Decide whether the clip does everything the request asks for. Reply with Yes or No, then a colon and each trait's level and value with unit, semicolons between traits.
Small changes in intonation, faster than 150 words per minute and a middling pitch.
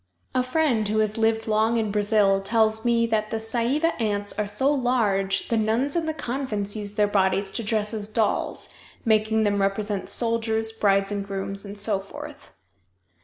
No: narrow, 2.2 semitones; average, 175 wpm; high, 215 Hz